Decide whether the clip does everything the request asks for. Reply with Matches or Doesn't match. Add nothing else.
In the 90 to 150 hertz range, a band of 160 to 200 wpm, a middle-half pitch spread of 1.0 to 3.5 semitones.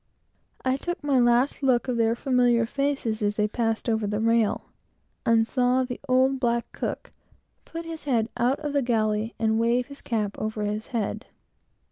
Doesn't match